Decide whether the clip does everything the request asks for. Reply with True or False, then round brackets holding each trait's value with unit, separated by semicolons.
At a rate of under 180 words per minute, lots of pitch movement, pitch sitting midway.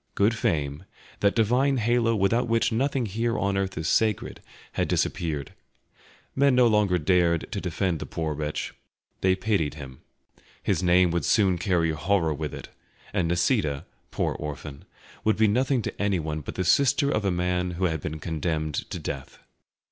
False (170 wpm; 5.8 semitones; 90 Hz)